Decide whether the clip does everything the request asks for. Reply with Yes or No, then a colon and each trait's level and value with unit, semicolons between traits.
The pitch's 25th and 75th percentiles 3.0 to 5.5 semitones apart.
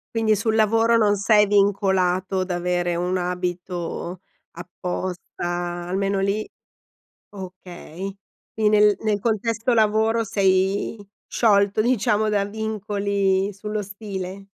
No: narrow, 2.6 semitones